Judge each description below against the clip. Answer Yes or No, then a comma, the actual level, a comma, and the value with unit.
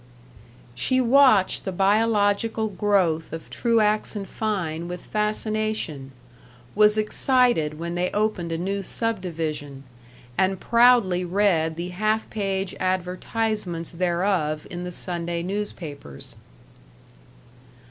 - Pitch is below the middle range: No, high, 190 Hz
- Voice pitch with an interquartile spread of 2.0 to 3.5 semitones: No, average, 3.9 semitones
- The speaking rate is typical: No, slow, 105 wpm